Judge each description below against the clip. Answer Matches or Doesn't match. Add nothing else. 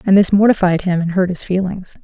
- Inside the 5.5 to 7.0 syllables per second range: Matches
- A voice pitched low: Doesn't match